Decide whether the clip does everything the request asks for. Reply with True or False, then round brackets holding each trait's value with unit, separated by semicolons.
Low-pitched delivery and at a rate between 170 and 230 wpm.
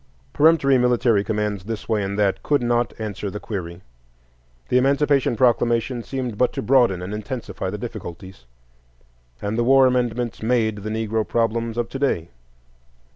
False (115 Hz; 155 wpm)